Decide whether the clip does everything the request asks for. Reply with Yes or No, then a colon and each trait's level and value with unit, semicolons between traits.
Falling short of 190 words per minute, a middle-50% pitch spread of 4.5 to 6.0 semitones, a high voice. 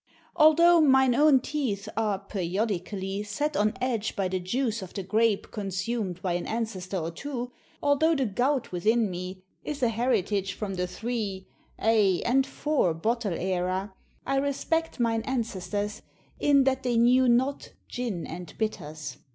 Yes: average, 150 wpm; wide, 5.5 semitones; high, 220 Hz